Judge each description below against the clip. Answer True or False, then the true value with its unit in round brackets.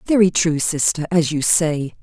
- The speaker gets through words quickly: False (180 wpm)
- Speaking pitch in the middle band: True (165 Hz)